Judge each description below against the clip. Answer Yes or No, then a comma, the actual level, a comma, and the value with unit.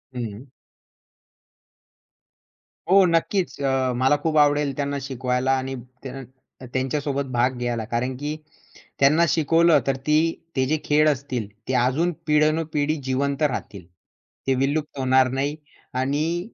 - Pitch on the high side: No, medium, 140 Hz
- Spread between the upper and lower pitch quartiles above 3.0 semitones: No, average, 2.7 semitones